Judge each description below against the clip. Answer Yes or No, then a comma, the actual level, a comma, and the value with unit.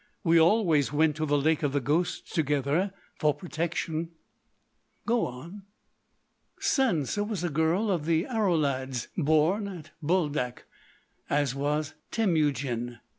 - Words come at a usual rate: No, slow, 115 wpm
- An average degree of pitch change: Yes, average, 4.0 semitones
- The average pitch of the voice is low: No, medium, 160 Hz